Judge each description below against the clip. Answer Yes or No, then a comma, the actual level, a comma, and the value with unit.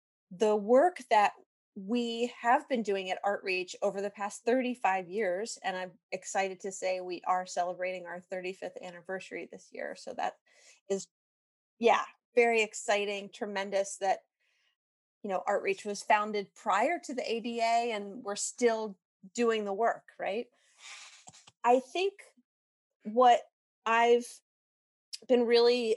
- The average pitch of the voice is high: Yes, high, 205 Hz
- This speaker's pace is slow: Yes, slow, 130 wpm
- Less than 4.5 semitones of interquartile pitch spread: Yes, average, 3.8 semitones